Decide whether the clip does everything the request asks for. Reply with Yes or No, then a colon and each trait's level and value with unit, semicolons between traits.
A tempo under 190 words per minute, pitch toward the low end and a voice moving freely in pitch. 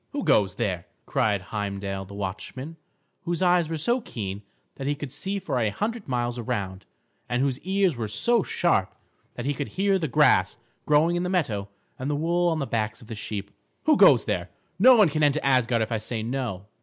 No: fast, 205 wpm; low, 130 Hz; wide, 8.3 semitones